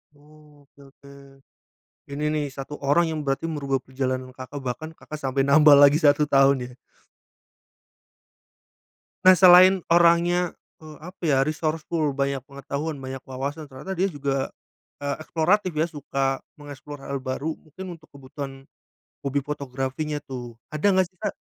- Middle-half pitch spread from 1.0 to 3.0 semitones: Yes, narrow, 2.6 semitones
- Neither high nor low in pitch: Yes, medium, 145 Hz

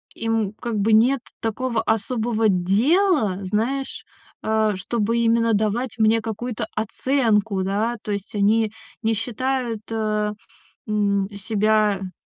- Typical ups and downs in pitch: No, narrow, 2.0 semitones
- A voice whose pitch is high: Yes, high, 220 Hz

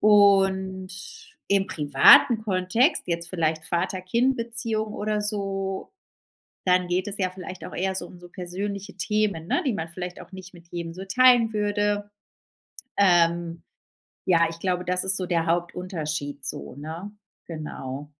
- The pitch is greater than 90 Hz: Yes, medium, 185 Hz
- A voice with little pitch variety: No, average, 3.2 semitones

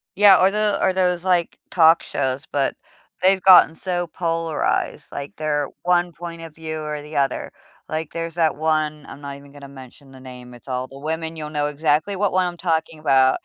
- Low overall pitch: No, medium, 160 Hz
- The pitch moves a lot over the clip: No, average, 3.5 semitones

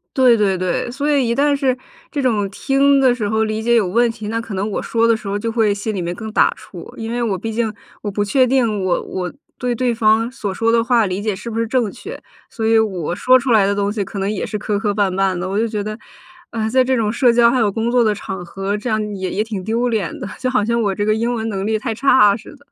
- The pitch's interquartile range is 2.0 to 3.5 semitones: Yes, average, 2.8 semitones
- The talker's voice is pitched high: Yes, high, 220 Hz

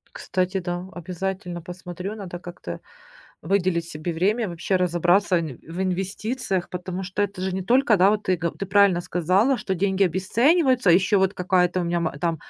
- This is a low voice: No, medium, 185 Hz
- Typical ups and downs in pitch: No, narrow, 2.1 semitones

